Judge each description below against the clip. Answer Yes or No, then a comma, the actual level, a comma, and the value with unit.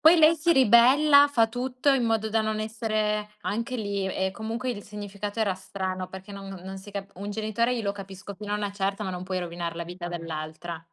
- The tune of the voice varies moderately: Yes, average, 3.1 semitones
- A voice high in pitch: Yes, high, 205 Hz